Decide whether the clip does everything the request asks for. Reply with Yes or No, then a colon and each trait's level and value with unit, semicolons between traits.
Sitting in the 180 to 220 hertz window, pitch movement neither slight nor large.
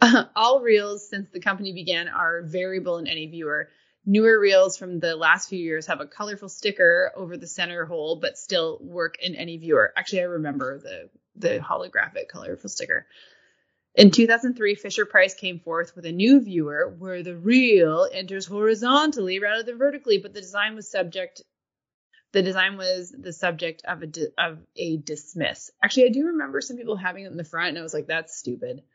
Yes: high, 190 Hz; average, 4.6 semitones